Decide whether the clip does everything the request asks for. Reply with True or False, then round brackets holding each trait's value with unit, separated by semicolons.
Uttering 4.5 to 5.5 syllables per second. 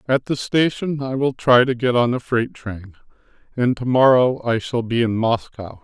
True (4.7 syllables/s)